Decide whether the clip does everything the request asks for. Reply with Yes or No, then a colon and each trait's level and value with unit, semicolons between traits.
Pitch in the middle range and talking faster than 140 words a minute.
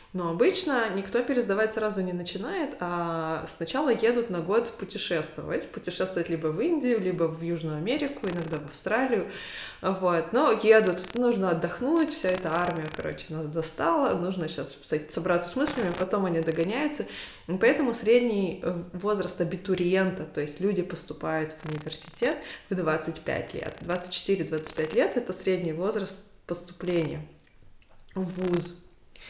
No: medium, 180 Hz; average, 135 wpm